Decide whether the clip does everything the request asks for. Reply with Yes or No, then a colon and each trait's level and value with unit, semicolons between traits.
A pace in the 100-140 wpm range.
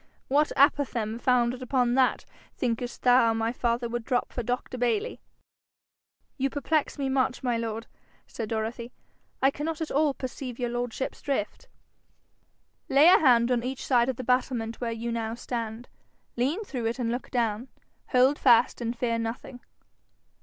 No: average, 160 wpm